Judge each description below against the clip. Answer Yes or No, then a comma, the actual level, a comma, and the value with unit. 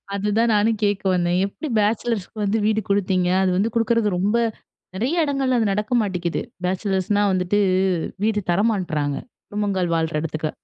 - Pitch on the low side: No, high, 205 Hz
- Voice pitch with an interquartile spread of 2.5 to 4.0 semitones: Yes, average, 3.3 semitones